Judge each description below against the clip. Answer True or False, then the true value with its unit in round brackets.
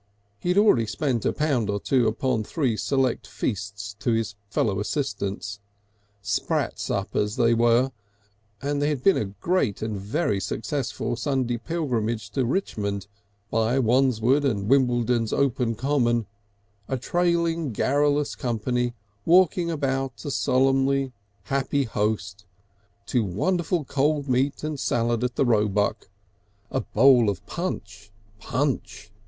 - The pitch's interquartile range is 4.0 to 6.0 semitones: True (4.6 semitones)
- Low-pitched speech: True (125 Hz)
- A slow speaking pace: True (130 wpm)